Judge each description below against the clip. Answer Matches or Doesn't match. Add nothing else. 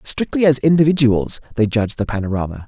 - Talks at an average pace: Matches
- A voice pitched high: Doesn't match